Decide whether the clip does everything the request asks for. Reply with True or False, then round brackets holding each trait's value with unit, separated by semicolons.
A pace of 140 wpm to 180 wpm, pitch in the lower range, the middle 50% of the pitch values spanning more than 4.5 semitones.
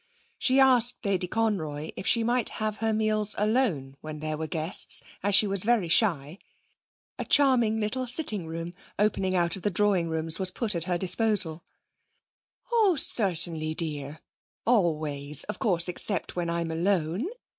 False (155 wpm; 190 Hz; 5.2 semitones)